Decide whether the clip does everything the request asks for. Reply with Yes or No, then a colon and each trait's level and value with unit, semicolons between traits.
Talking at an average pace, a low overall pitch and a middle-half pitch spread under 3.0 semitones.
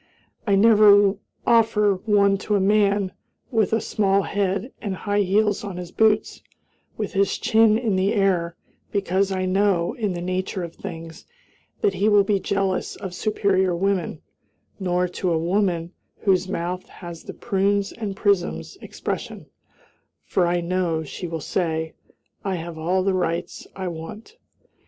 No: average, 155 wpm; high, 195 Hz; narrow, 2.5 semitones